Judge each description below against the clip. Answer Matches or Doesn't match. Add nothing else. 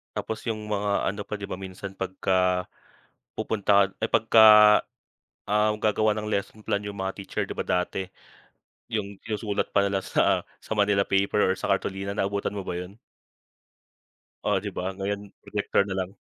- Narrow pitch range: Matches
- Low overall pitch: Matches